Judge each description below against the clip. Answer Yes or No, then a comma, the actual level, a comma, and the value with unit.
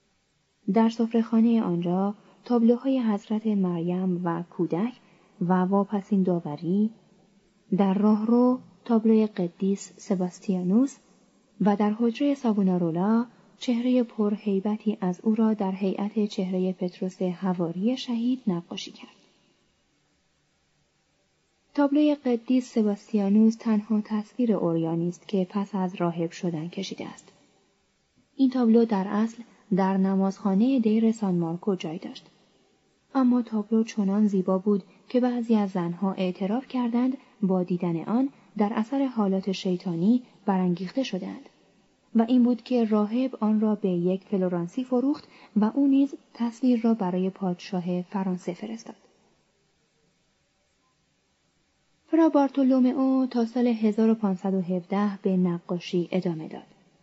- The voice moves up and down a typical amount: Yes, average, 3.8 semitones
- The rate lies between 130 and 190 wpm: No, average, 115 wpm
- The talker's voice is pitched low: No, high, 205 Hz